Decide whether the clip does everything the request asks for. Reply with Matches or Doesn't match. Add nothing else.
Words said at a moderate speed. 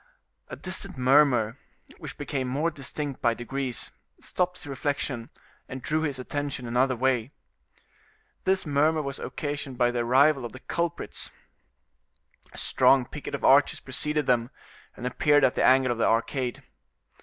Matches